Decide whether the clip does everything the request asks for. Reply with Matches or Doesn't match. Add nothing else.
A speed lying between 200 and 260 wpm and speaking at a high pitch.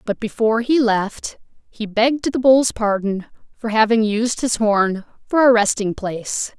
Doesn't match